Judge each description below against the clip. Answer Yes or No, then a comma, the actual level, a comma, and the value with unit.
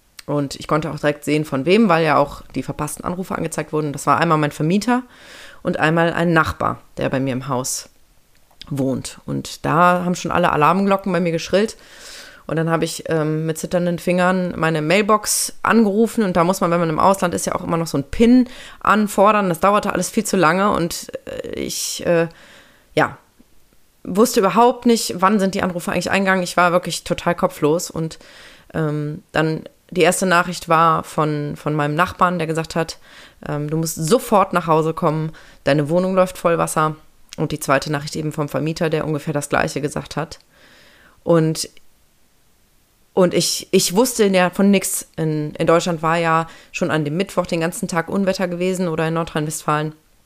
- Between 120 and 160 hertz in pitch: No, medium, 170 Hz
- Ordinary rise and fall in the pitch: Yes, average, 3.3 semitones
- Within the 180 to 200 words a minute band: Yes, average, 185 wpm